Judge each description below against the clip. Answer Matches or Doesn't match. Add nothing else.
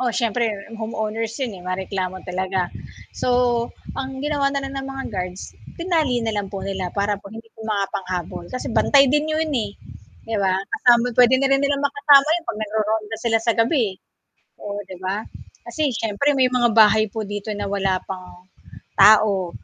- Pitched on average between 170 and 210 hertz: Doesn't match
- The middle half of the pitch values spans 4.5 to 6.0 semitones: Matches